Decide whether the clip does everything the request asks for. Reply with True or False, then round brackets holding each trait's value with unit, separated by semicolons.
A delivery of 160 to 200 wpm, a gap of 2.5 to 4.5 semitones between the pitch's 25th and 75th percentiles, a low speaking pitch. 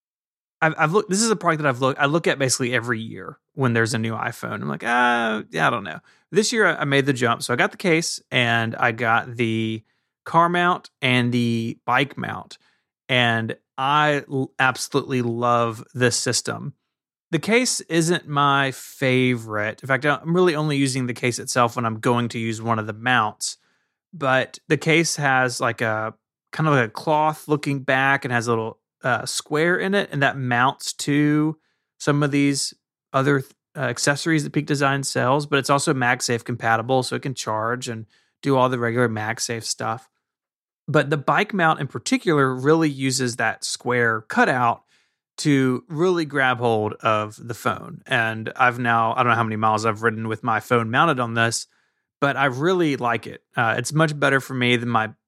True (195 wpm; 4.2 semitones; 130 Hz)